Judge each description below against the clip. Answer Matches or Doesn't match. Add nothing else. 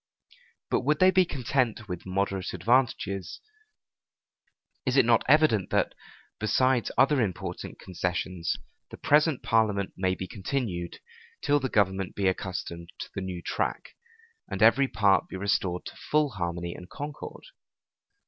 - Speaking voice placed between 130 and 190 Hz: Doesn't match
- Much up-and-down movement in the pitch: Matches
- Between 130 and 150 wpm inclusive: Matches